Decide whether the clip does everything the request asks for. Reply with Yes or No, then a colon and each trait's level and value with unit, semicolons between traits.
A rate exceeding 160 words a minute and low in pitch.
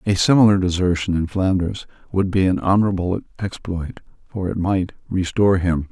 No: average, 150 wpm; very low, 95 Hz